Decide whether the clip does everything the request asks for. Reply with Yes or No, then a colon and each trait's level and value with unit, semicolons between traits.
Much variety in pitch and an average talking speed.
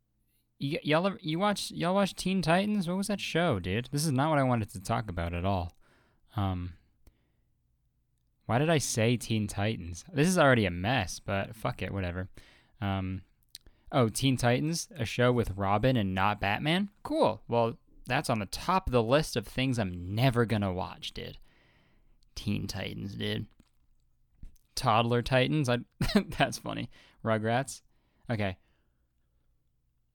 Yes: wide, 6.2 semitones; average, 155 wpm